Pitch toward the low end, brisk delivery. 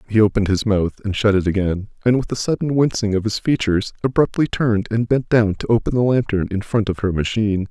Yes: low, 110 Hz; fast, 235 wpm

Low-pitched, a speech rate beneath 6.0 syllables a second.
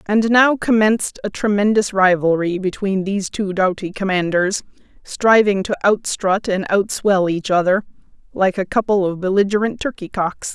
No: high, 195 Hz; 4.8 syllables/s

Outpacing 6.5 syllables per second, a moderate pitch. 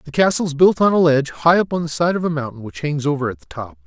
Yes: 6.8 syllables/s; medium, 160 Hz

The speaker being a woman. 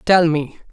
No: male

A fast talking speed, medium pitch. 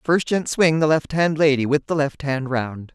Yes: fast, 245 wpm; medium, 145 Hz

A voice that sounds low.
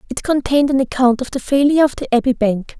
No: very high, 260 Hz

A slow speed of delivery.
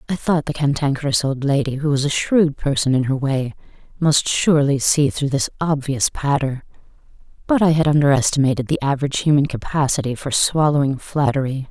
No: average, 170 wpm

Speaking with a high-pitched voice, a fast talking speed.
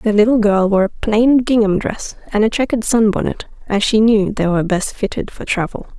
Yes: high, 215 Hz; fast, 210 wpm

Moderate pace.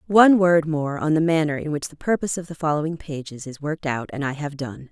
No: fast, 245 wpm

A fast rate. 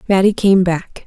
No: average, 170 wpm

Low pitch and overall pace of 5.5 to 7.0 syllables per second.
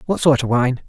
Yes: low, 130 Hz; 5.6 syllables/s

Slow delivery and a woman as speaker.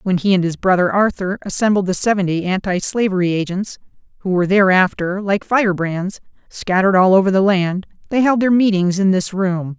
No: average, 180 wpm; female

